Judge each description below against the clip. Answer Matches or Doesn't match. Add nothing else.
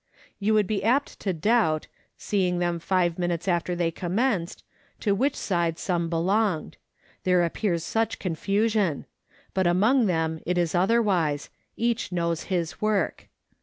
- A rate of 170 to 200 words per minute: Doesn't match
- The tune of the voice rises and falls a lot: Doesn't match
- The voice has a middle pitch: Matches